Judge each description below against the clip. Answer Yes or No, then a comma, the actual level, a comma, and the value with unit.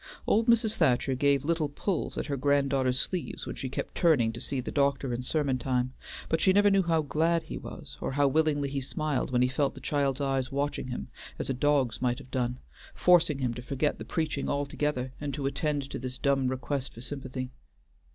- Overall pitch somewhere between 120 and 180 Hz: Yes, medium, 140 Hz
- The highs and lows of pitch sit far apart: No, average, 2.8 semitones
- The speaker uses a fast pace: Yes, fast, 210 wpm